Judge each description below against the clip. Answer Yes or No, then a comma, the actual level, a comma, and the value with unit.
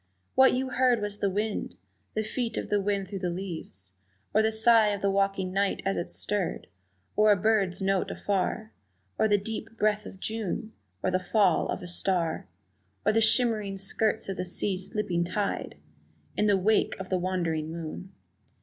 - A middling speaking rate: Yes, average, 185 wpm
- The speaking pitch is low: No, high, 200 Hz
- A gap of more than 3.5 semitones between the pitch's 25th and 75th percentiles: No, average, 2.7 semitones